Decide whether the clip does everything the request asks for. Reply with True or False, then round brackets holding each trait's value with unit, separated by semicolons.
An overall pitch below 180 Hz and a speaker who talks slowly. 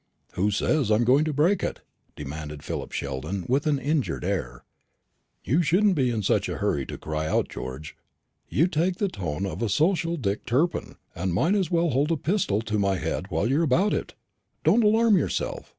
False (135 Hz; 200 wpm)